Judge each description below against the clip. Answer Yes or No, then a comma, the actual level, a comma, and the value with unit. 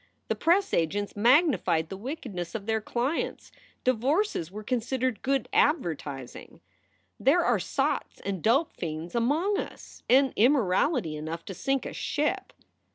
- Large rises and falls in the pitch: Yes, wide, 7.5 semitones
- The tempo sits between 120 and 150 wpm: Yes, slow, 135 wpm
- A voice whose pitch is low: No, high, 235 Hz